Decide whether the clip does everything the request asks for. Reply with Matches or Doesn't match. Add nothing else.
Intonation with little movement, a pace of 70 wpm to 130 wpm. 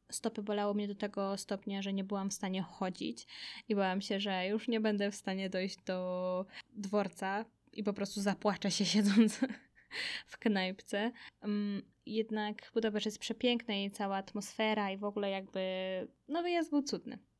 Doesn't match